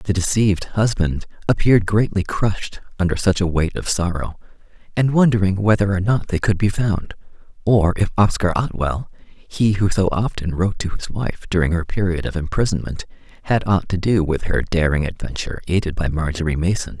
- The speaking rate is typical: Yes, average, 175 wpm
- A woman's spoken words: No, male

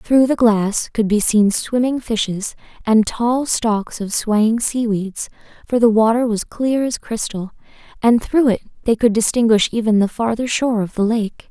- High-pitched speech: Yes, high, 225 Hz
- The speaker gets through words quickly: No, average, 175 wpm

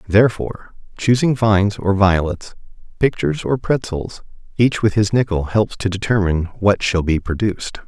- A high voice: No, low, 100 Hz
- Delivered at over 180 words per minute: No, average, 145 wpm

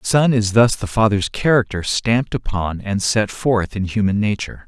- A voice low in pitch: Yes, low, 105 Hz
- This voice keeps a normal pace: Yes, average, 195 wpm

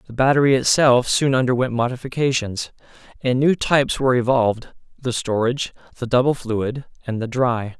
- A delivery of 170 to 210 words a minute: No, average, 140 wpm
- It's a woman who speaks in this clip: No, male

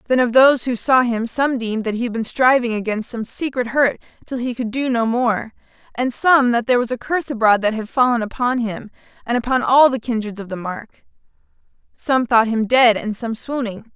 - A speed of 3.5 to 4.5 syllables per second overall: No, 5.4 syllables/s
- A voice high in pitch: Yes, high, 235 Hz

